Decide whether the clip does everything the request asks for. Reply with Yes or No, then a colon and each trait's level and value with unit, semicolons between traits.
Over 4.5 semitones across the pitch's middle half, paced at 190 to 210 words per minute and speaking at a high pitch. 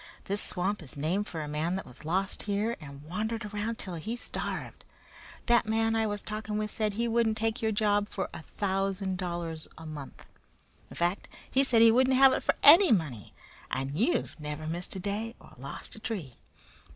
Yes: average, 5.1 semitones; average, 200 wpm; high, 205 Hz